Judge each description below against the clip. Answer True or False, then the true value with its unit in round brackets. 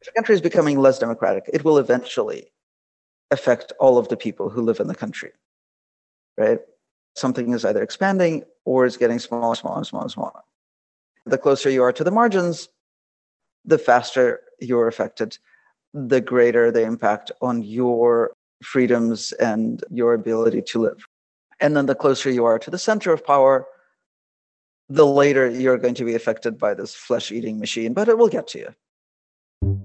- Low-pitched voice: True (130 Hz)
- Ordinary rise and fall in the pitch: False (6.4 semitones)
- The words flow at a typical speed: True (165 wpm)